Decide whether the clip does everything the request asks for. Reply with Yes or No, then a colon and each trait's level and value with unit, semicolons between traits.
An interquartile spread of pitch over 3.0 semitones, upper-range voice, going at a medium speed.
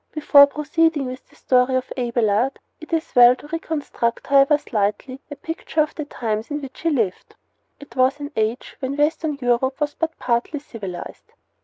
Yes: average, 3.6 semitones; very high, 270 Hz; average, 175 wpm